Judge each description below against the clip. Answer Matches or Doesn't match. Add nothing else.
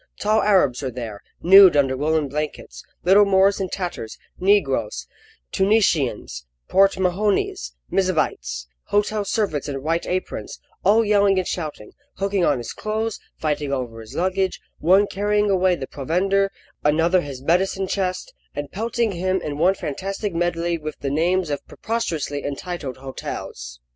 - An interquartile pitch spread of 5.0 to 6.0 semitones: Matches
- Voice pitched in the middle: Matches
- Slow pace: Doesn't match